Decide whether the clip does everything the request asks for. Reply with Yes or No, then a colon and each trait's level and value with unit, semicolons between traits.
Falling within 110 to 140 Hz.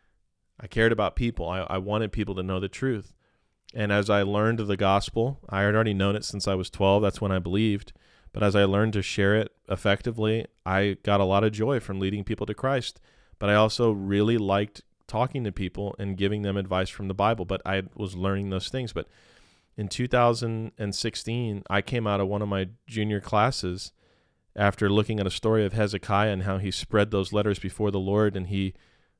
No: low, 100 Hz